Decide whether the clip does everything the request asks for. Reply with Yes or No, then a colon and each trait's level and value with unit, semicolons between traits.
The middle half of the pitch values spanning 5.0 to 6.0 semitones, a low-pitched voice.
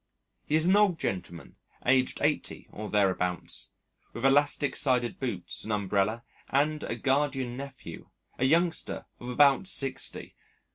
Yes: wide, 5.4 semitones; low, 130 Hz